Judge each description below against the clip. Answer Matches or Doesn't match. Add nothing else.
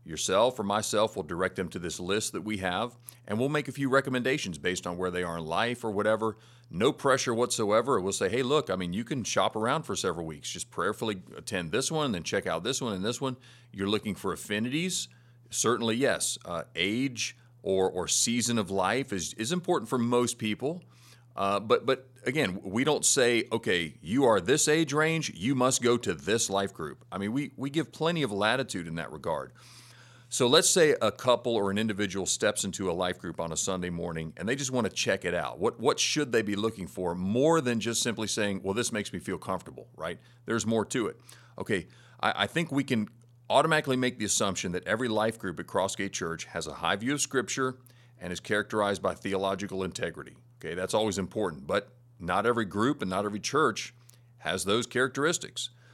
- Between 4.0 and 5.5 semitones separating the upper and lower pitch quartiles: Matches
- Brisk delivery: Matches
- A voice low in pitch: Matches